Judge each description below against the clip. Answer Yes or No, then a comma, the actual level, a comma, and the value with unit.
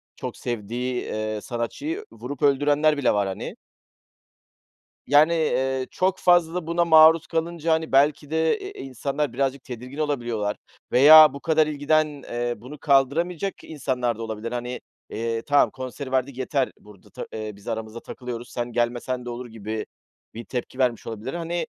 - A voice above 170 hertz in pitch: No, low, 130 Hz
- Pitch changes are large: No, average, 4.6 semitones